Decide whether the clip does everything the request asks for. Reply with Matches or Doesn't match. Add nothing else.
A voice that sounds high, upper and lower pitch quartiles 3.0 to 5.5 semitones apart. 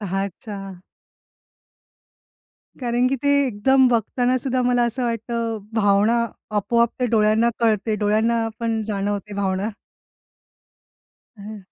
Doesn't match